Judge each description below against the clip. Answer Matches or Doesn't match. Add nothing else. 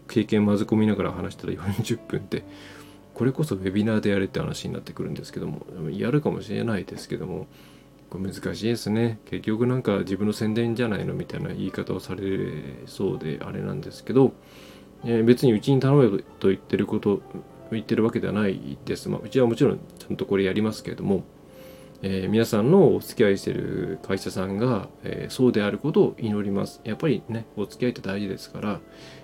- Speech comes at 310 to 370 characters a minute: Doesn't match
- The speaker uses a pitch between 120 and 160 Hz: Doesn't match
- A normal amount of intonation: Matches